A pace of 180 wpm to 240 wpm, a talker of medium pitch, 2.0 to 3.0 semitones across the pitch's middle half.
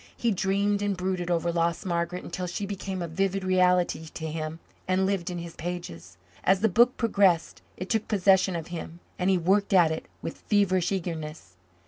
Yes: average, 185 wpm; medium, 180 Hz; narrow, 2.4 semitones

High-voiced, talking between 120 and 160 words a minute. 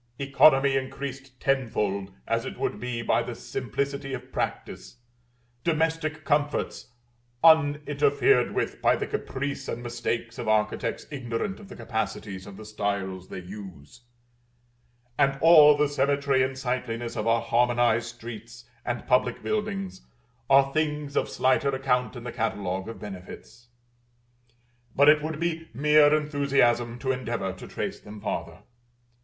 No: low, 130 Hz; average, 140 wpm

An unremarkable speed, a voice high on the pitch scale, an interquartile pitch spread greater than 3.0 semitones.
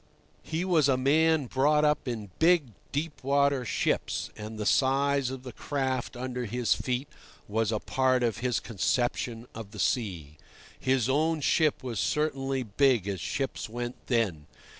No: average, 160 wpm; low, 130 Hz; average, 3.7 semitones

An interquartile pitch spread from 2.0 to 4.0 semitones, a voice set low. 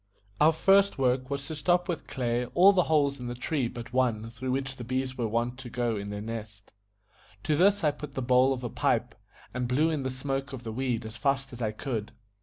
Yes: average, 3.1 semitones; low, 130 Hz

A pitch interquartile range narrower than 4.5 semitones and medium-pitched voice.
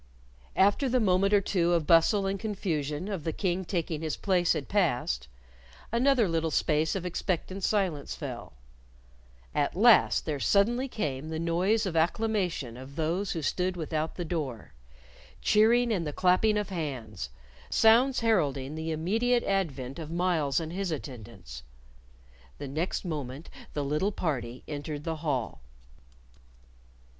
No: average, 5.0 semitones; medium, 170 Hz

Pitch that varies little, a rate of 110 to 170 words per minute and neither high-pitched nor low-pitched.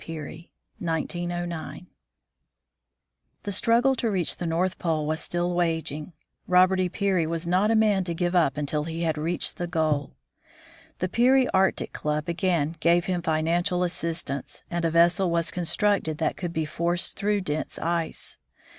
Yes: narrow, 2.2 semitones; average, 155 wpm; medium, 170 Hz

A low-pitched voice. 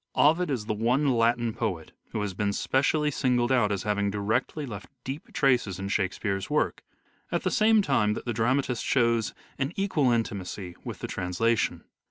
Yes: low, 115 Hz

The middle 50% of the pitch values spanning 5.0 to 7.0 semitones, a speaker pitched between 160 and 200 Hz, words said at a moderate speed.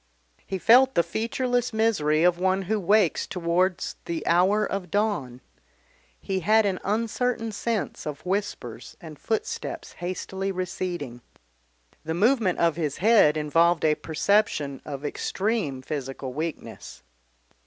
No: average, 5.3 semitones; medium, 185 Hz; slow, 125 wpm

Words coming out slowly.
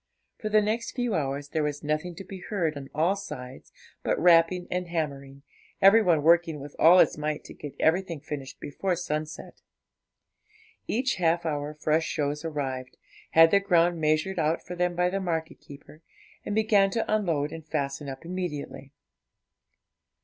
No: average, 165 wpm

